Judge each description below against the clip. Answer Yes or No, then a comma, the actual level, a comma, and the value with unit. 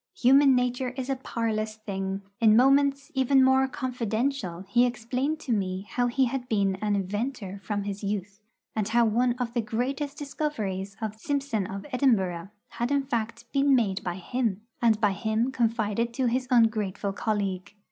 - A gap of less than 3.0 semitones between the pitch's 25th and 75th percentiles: No, average, 4.2 semitones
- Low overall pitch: No, high, 230 Hz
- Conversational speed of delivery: Yes, average, 165 wpm